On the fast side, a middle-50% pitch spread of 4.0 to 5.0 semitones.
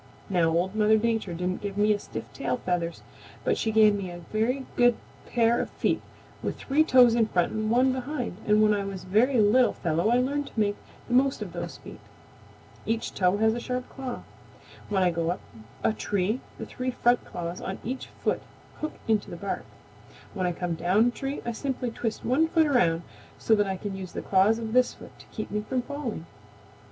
Yes: fast, 210 wpm; average, 4.6 semitones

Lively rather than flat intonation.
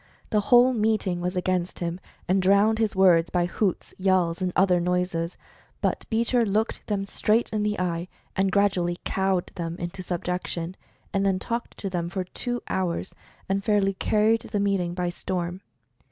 No: average, 2.8 semitones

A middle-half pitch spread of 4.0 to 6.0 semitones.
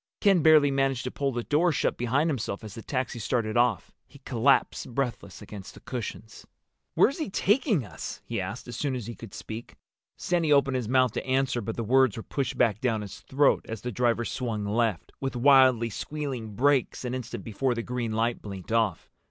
No: average, 3.3 semitones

